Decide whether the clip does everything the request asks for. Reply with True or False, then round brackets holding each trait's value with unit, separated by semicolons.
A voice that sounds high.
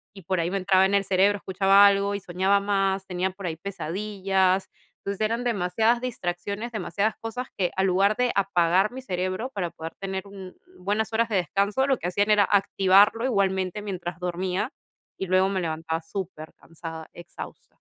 True (195 Hz)